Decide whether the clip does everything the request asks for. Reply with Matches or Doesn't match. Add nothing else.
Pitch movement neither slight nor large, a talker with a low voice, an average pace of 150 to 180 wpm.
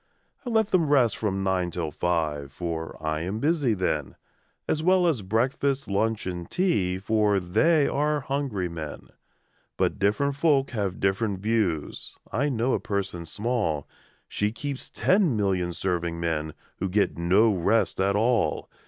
Doesn't match